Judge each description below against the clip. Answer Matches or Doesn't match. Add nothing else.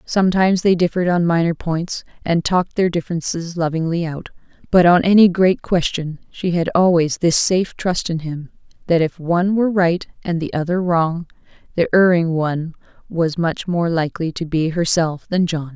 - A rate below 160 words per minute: Doesn't match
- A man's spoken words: Doesn't match